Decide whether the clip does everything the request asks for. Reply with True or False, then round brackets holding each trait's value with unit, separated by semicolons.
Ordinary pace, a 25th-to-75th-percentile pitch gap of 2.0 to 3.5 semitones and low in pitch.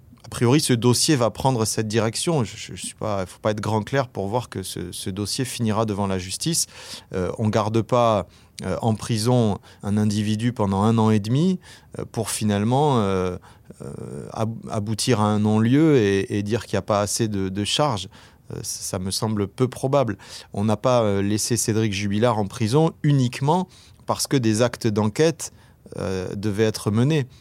True (185 wpm; 3.1 semitones; 110 Hz)